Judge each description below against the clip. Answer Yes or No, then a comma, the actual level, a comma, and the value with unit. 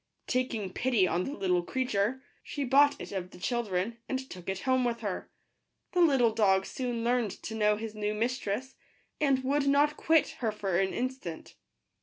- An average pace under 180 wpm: No, average, 185 wpm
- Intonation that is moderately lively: Yes, average, 4.8 semitones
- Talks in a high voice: Yes, high, 235 Hz